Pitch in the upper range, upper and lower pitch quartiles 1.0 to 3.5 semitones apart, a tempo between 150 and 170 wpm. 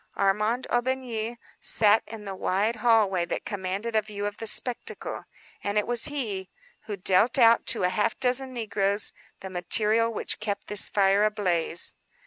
Yes: high, 210 Hz; average, 2.7 semitones; average, 160 wpm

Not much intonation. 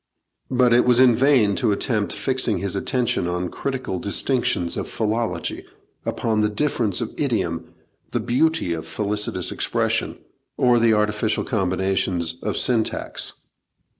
No: average, 4.2 semitones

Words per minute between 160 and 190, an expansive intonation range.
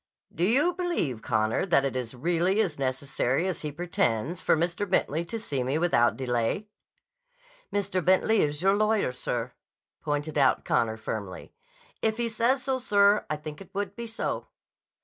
Yes: average, 170 wpm; wide, 7.5 semitones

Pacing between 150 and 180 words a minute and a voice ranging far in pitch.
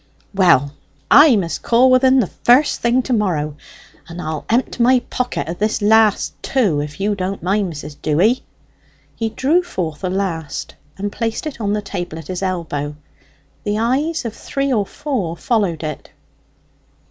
Yes: average, 170 wpm; wide, 6.3 semitones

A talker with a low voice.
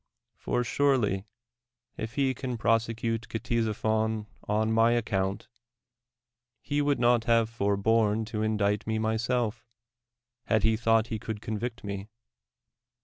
Yes: low, 110 Hz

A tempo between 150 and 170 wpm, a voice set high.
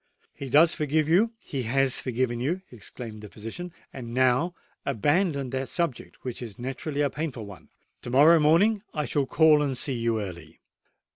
No: average, 165 wpm; low, 135 Hz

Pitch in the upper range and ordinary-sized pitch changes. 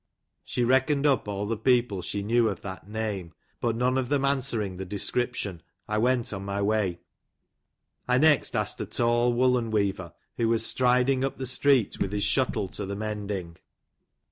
No: low, 115 Hz; average, 4.0 semitones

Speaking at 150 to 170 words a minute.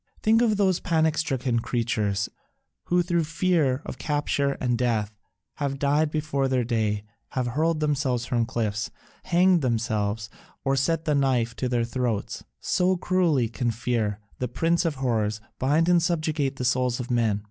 Yes: average, 160 wpm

